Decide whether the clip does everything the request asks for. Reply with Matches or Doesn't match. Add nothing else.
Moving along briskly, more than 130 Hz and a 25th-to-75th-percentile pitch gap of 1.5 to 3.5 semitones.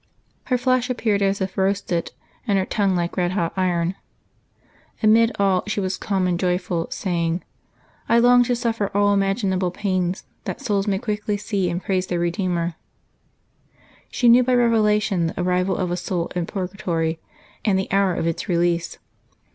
Doesn't match